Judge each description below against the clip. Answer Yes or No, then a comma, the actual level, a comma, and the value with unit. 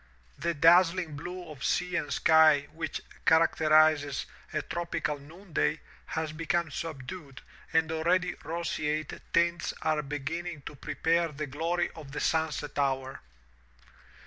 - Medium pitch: Yes, medium, 160 Hz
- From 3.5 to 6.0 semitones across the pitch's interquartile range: No, narrow, 2.4 semitones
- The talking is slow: Yes, slow, 125 wpm